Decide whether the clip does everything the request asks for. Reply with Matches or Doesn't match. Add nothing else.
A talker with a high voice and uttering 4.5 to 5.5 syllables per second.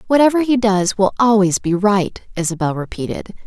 Matches